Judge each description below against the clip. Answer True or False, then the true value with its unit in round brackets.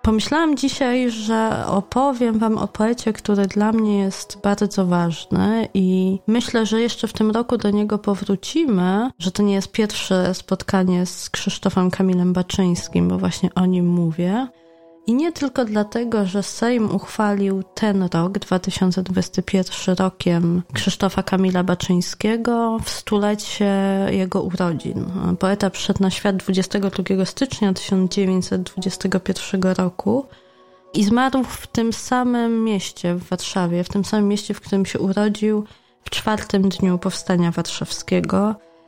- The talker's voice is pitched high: True (195 Hz)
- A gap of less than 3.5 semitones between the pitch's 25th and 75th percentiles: True (2.7 semitones)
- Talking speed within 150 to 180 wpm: False (130 wpm)